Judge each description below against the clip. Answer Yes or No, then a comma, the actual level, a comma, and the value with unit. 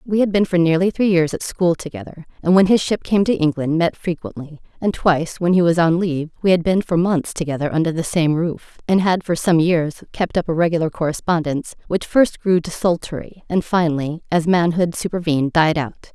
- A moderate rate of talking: No, fast, 210 wpm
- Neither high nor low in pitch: Yes, medium, 170 Hz